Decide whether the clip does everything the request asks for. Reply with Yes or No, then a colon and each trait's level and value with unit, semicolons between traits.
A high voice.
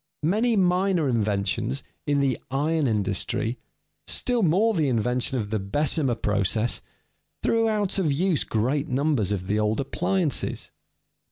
No: medium, 140 Hz